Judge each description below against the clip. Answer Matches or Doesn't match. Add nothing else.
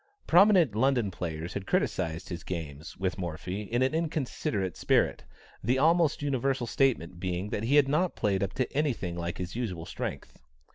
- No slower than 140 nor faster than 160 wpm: Doesn't match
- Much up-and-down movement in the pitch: Matches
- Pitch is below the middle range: Matches